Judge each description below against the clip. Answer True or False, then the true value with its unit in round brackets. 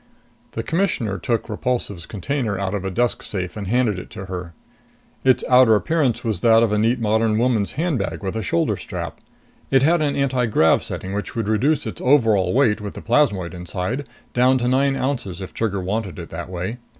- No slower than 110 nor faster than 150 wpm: False (195 wpm)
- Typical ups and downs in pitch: True (4.7 semitones)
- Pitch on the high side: False (110 Hz)